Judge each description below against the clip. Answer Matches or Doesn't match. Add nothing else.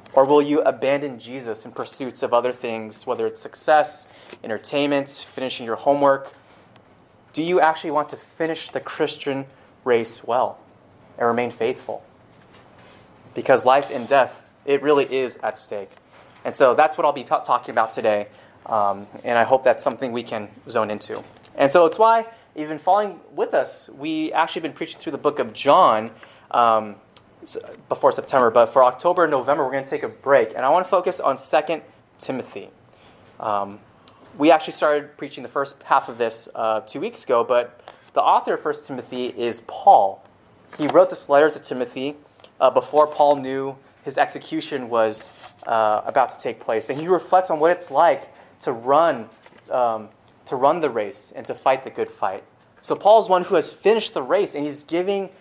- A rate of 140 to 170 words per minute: Doesn't match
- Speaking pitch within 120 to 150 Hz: Matches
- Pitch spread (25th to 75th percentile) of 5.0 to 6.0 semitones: Matches